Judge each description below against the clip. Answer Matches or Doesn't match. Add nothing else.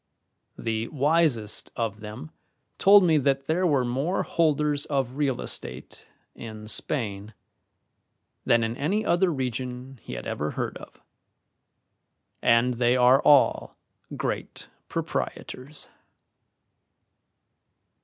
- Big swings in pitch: Doesn't match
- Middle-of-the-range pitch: Doesn't match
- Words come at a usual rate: Doesn't match